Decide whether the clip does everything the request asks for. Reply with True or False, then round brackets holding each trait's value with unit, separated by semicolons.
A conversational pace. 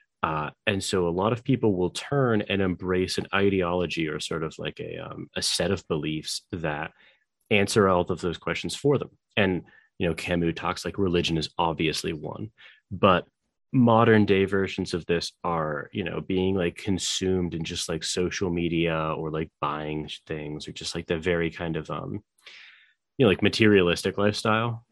True (180 wpm)